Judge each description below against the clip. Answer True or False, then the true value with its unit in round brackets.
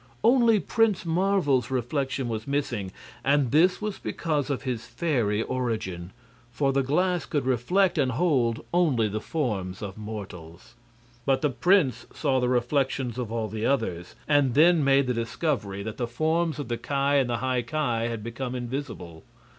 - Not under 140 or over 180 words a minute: True (165 wpm)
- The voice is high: False (130 Hz)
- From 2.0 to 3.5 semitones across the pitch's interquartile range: False (4.5 semitones)